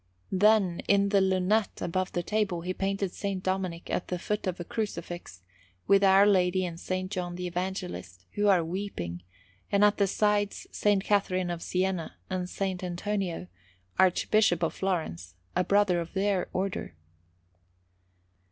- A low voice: No, medium, 185 Hz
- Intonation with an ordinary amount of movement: No, narrow, 2.2 semitones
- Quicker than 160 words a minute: No, average, 150 wpm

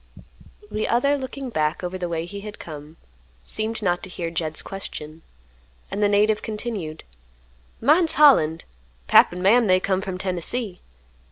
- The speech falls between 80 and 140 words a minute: No, average, 155 wpm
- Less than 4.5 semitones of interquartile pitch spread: No, average, 4.8 semitones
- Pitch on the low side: No, high, 195 Hz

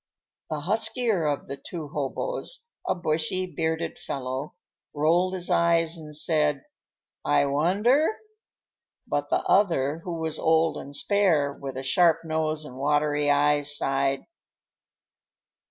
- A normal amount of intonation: Yes, average, 3.2 semitones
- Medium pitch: Yes, medium, 155 Hz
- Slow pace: Yes, slow, 125 wpm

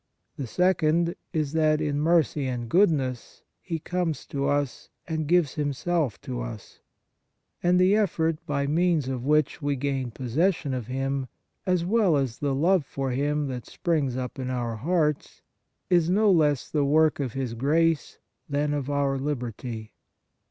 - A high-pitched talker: No, medium, 145 Hz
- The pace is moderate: Yes, average, 165 wpm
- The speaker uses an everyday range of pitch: Yes, average, 3.8 semitones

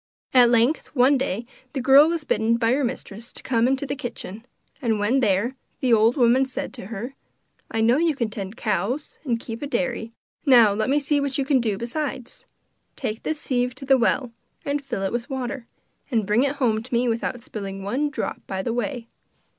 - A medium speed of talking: No, fast, 210 wpm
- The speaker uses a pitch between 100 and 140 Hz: No, high, 245 Hz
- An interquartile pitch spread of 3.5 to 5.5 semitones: No, average, 3.1 semitones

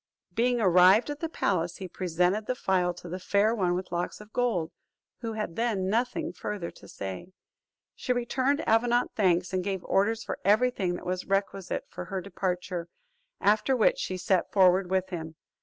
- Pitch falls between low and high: No, high, 195 Hz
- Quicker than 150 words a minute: Yes, average, 180 wpm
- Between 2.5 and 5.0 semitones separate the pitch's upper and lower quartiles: Yes, average, 3.9 semitones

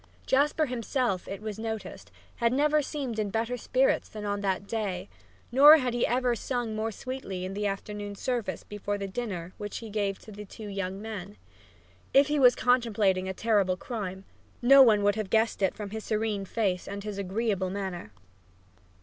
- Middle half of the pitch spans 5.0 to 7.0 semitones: No, average, 3.5 semitones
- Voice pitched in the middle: No, high, 215 Hz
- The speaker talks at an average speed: Yes, average, 185 wpm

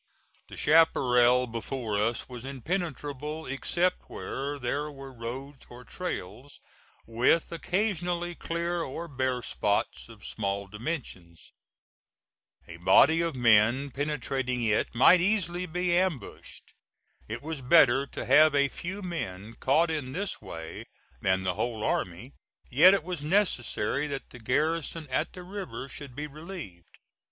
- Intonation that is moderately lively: No, wide, 5.7 semitones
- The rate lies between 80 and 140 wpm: Yes, slow, 135 wpm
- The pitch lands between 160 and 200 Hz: No, medium, 140 Hz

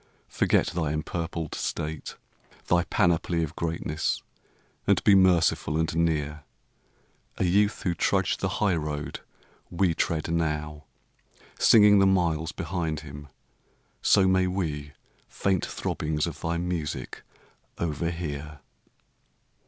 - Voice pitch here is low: Yes, very low, 80 Hz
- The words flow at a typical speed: No, slow, 110 wpm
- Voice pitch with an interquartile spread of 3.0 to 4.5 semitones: No, narrow, 2.5 semitones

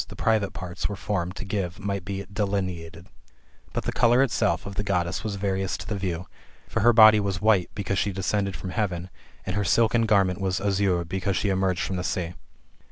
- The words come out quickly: Yes, fast, 210 wpm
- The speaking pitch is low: Yes, very low, 95 Hz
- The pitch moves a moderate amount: No, narrow, 1.9 semitones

